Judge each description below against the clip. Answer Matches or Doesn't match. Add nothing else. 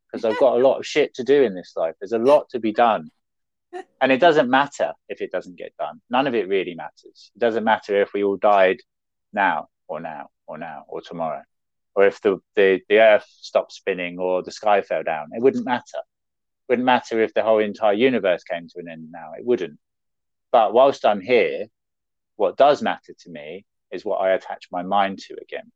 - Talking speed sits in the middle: Doesn't match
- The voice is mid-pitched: Doesn't match